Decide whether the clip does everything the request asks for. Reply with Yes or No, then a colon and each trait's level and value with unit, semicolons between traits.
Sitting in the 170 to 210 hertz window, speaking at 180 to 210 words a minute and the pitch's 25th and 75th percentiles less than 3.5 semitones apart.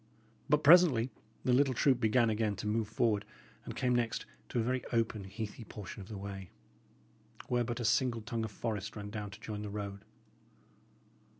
No: low, 110 Hz; average, 185 wpm; average, 2.8 semitones